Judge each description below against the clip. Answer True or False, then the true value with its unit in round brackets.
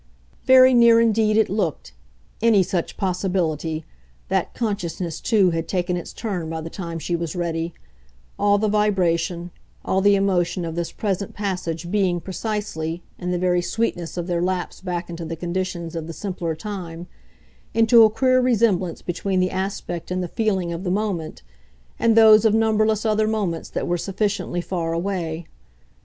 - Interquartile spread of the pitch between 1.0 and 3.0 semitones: False (3.7 semitones)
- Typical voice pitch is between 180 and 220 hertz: True (185 Hz)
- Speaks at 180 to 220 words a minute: False (165 wpm)